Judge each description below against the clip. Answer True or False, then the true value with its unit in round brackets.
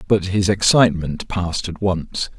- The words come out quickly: False (150 wpm)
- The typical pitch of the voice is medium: False (95 Hz)